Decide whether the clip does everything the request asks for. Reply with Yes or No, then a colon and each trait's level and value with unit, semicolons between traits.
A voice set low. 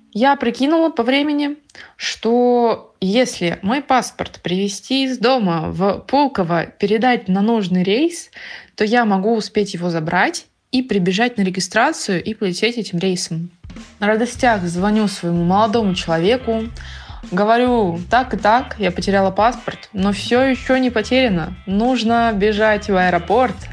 No: high, 215 Hz